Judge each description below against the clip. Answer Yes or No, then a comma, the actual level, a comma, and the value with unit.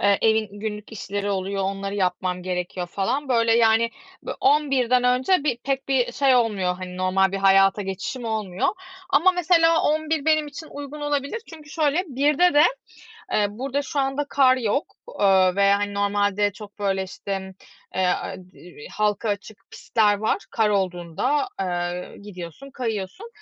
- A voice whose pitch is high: Yes, high, 215 Hz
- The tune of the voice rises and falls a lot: Yes, wide, 6.1 semitones